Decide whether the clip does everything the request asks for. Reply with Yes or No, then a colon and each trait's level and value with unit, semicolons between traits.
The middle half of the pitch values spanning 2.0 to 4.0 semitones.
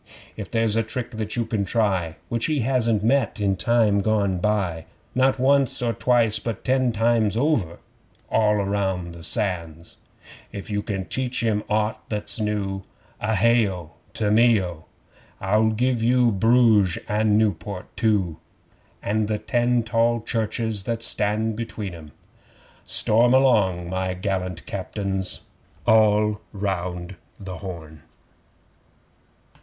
Yes: average, 3.2 semitones